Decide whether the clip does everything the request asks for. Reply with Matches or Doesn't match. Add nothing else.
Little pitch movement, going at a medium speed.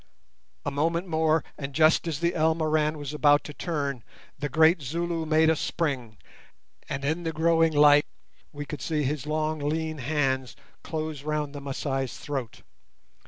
Matches